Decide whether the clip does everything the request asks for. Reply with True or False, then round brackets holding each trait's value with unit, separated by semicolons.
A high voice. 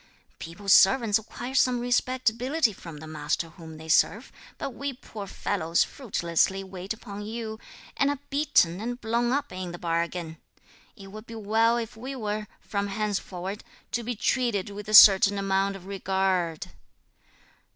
True (205 Hz)